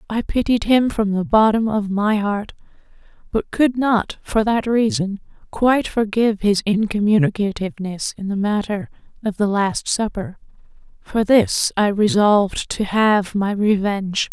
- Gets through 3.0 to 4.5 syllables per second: Yes, 4.4 syllables/s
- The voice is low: No, high, 210 Hz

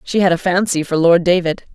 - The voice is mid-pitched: Yes, medium, 175 Hz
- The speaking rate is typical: No, fast, 240 wpm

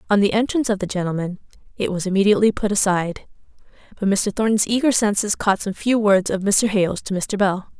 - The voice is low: No, high, 200 Hz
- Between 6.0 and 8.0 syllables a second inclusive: Yes, 6.2 syllables/s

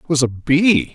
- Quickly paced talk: Yes, fast, 255 wpm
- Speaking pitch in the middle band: Yes, medium, 145 Hz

